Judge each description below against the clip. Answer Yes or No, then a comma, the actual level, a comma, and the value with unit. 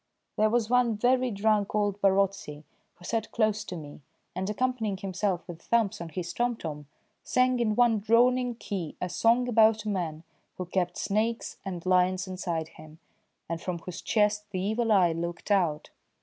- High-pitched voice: Yes, high, 200 Hz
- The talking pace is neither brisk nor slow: Yes, average, 170 wpm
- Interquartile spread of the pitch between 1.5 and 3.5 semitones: No, average, 4.1 semitones